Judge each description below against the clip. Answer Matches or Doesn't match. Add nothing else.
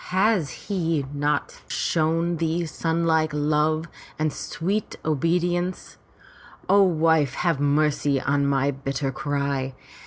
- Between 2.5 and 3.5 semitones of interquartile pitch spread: Matches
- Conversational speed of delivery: Doesn't match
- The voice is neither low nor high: Matches